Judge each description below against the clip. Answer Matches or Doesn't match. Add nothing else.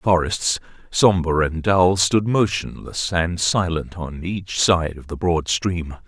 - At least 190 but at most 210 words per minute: Doesn't match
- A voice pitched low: Matches